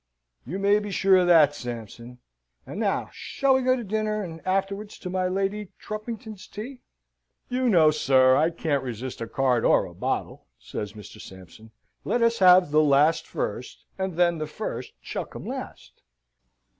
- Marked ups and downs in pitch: Yes, wide, 7.2 semitones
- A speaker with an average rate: Yes, average, 170 wpm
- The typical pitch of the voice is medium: Yes, medium, 180 Hz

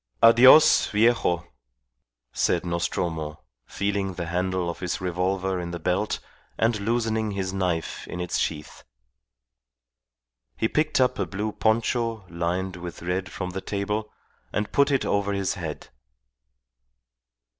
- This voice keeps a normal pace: No, slow, 130 wpm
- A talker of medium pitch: No, very low, 95 Hz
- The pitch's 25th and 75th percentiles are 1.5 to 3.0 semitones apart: No, average, 3.6 semitones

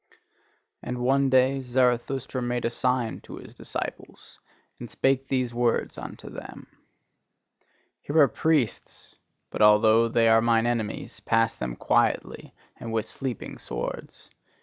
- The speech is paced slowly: Yes, slow, 130 wpm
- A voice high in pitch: No, low, 120 Hz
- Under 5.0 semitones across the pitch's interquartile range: Yes, narrow, 2.5 semitones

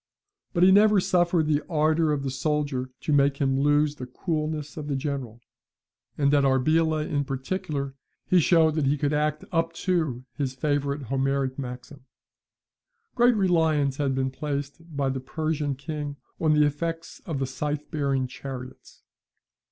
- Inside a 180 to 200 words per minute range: No, average, 160 wpm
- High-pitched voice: No, medium, 145 Hz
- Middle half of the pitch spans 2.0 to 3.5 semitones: Yes, narrow, 2.6 semitones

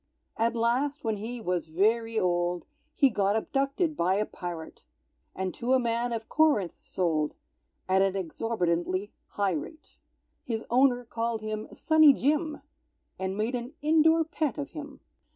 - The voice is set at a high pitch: Yes, high, 225 Hz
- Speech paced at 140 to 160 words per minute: Yes, average, 150 wpm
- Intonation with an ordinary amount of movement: No, wide, 6.4 semitones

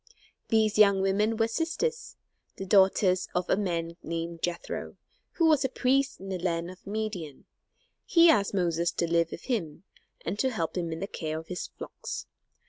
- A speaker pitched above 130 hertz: Yes, high, 190 Hz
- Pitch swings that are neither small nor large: Yes, average, 4.7 semitones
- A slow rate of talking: No, average, 180 wpm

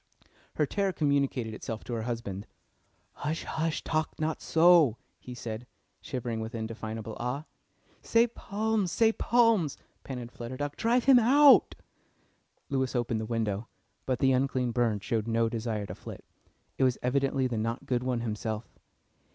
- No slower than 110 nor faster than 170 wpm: Yes, average, 150 wpm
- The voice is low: Yes, low, 125 Hz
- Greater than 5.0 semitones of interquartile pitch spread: Yes, wide, 5.4 semitones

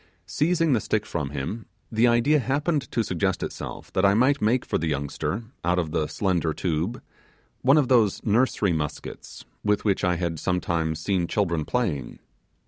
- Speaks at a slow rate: No, average, 170 wpm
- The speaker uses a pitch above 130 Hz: No, low, 100 Hz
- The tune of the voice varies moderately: No, wide, 6.4 semitones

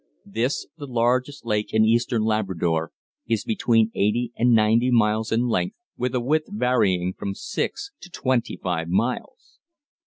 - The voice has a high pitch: No, low, 115 Hz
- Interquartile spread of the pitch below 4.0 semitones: Yes, average, 2.9 semitones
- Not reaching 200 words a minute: Yes, average, 150 wpm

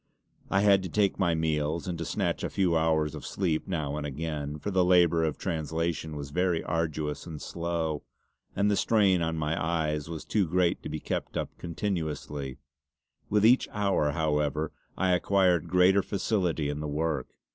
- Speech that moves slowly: No, average, 180 wpm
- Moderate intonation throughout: Yes, average, 3.3 semitones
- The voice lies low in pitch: Yes, very low, 80 Hz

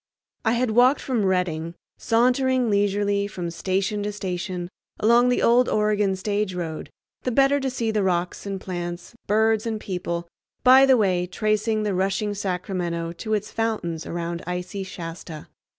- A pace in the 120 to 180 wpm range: Yes, average, 155 wpm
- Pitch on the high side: Yes, high, 200 Hz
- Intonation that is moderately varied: Yes, average, 3.8 semitones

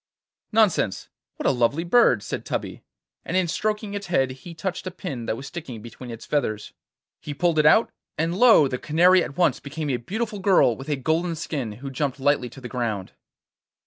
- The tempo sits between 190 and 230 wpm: Yes, average, 200 wpm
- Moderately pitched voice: Yes, medium, 150 Hz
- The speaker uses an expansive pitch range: Yes, wide, 6.1 semitones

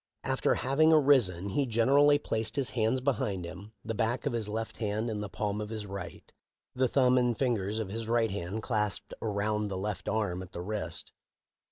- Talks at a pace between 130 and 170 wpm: No, average, 195 wpm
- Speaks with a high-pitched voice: No, low, 110 Hz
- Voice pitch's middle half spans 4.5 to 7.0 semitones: No, average, 3.3 semitones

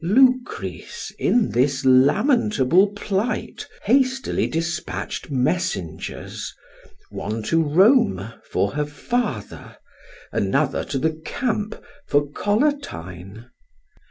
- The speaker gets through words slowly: Yes, slow, 85 wpm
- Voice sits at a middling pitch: Yes, medium, 160 Hz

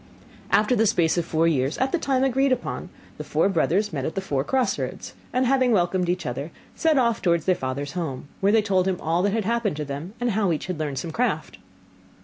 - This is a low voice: No, medium, 185 Hz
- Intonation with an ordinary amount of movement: No, wide, 6.6 semitones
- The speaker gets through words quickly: Yes, fast, 235 wpm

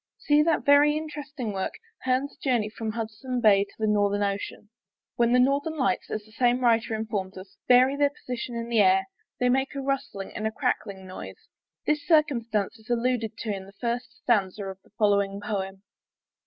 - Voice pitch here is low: No, high, 230 Hz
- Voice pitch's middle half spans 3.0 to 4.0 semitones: No, average, 4.4 semitones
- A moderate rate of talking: Yes, average, 185 wpm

